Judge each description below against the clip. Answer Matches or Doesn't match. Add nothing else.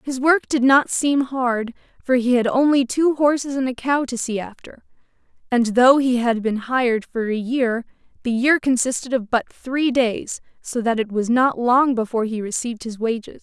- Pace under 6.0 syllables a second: Matches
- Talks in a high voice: Matches